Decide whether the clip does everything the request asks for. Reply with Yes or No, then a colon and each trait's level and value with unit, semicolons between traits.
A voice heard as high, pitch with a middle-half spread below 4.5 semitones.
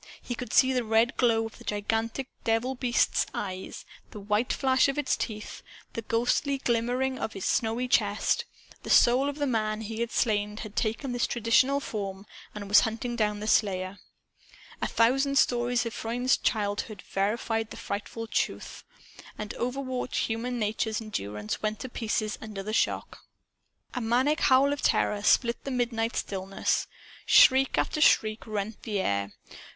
Yes: high, 225 Hz; average, 2.9 semitones